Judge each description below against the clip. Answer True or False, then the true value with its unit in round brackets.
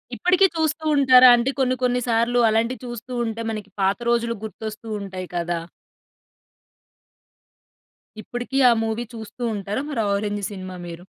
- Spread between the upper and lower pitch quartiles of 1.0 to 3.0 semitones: False (3.4 semitones)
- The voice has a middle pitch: False (230 Hz)